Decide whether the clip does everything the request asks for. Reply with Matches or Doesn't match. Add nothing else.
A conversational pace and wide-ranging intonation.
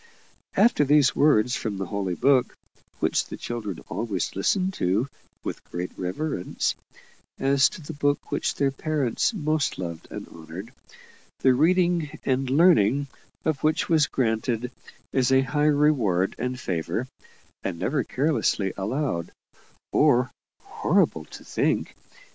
Doesn't match